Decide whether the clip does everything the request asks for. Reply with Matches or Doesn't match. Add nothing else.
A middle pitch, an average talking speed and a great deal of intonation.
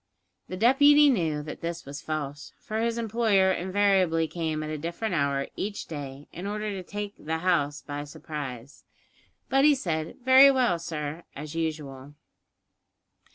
Matches